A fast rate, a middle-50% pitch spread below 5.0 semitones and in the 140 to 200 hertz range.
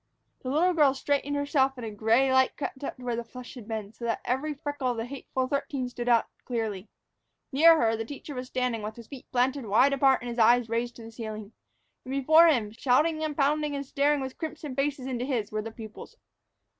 No: fast, 225 wpm; average, 3.6 semitones; very high, 255 Hz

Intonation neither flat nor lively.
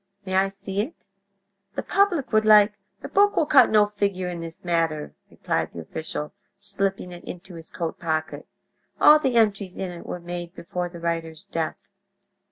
Yes: average, 3.7 semitones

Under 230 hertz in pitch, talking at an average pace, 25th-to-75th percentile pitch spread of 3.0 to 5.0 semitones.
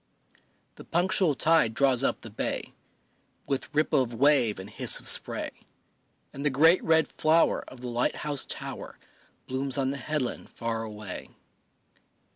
Yes: low, 135 Hz; average, 150 wpm; average, 4.3 semitones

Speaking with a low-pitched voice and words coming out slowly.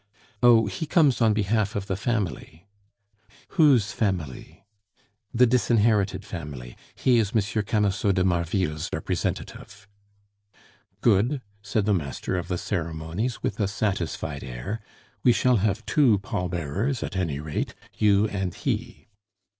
Yes: low, 100 Hz; slow, 130 wpm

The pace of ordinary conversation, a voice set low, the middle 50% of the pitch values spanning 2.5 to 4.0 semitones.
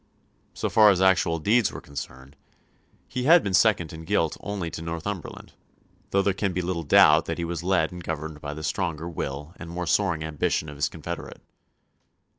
Yes: average, 190 wpm; very low, 85 Hz; average, 3.5 semitones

